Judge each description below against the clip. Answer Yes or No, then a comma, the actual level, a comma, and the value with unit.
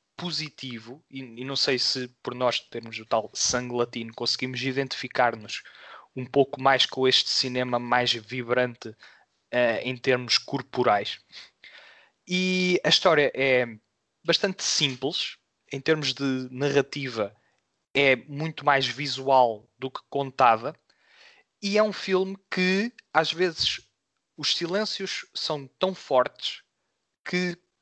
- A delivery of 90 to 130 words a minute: Yes, average, 125 wpm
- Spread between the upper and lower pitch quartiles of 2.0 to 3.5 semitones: No, average, 4.6 semitones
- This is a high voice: No, low, 135 Hz